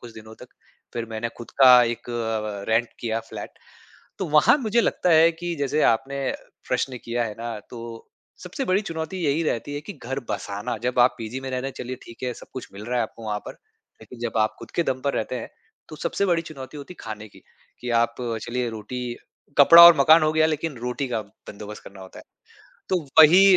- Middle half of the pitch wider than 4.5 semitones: Yes, average, 5.1 semitones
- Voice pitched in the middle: No, low, 125 Hz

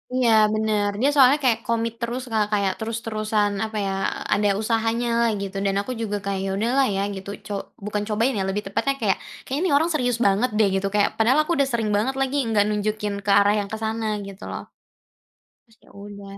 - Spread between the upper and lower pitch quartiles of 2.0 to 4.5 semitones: Yes, average, 2.7 semitones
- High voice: Yes, high, 220 Hz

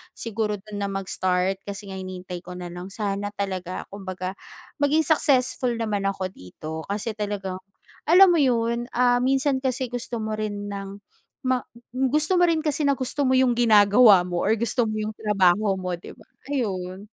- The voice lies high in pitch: Yes, high, 210 Hz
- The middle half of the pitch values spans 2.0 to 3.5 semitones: No, average, 4.7 semitones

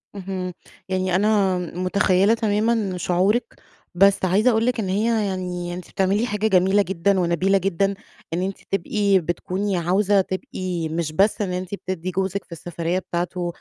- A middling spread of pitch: No, narrow, 2.1 semitones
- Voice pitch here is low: No, high, 190 Hz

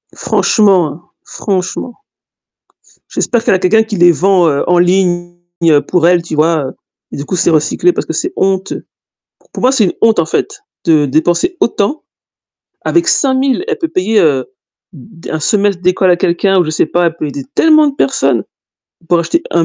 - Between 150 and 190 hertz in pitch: Yes, medium, 185 Hz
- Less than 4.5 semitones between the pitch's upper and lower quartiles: No, average, 4.9 semitones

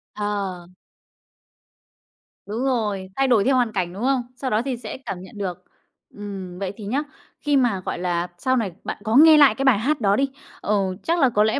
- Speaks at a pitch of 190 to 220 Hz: Yes, high, 215 Hz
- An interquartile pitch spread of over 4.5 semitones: Yes, average, 5.2 semitones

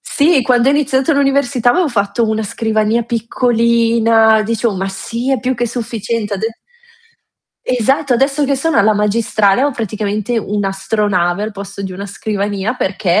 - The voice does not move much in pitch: No, average, 3.4 semitones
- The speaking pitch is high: Yes, high, 225 Hz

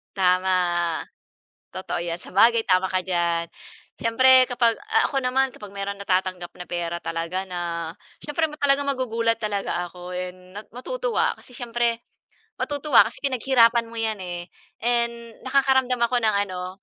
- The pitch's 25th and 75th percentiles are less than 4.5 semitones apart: No, average, 5.3 semitones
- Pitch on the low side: No, high, 215 Hz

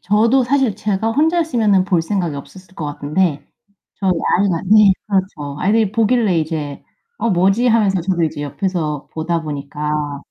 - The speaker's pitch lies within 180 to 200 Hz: Yes, high, 190 Hz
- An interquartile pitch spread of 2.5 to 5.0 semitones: No, wide, 5.6 semitones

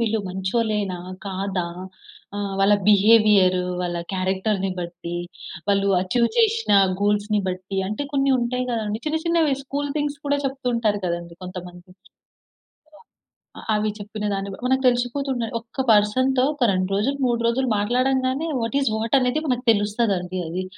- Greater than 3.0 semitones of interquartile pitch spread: Yes, average, 4.8 semitones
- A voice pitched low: No, high, 215 Hz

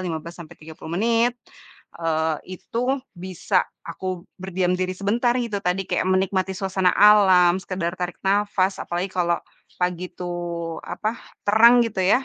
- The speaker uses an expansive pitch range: No, narrow, 2.4 semitones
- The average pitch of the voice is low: No, medium, 185 Hz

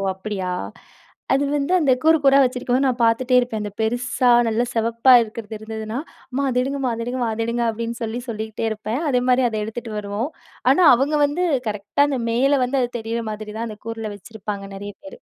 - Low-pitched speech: No, high, 230 Hz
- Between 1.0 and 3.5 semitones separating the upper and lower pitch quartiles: Yes, average, 2.9 semitones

